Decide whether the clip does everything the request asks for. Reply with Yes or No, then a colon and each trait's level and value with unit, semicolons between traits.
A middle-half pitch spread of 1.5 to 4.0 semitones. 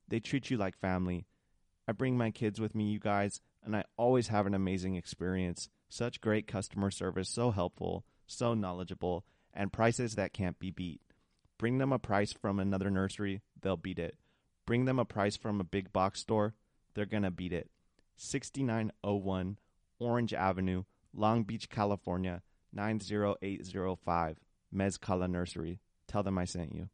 Yes: average, 2.9 semitones